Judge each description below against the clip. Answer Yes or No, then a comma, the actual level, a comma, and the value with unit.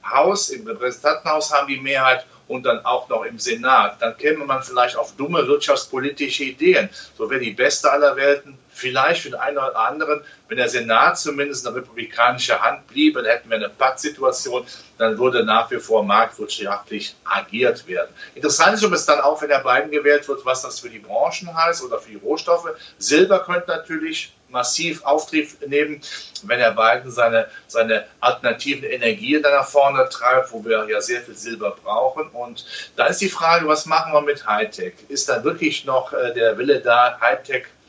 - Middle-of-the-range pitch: Yes, medium, 150 Hz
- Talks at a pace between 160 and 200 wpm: Yes, average, 185 wpm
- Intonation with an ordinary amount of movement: Yes, average, 4.6 semitones